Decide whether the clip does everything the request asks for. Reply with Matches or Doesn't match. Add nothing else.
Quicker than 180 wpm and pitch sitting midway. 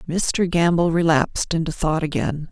Doesn't match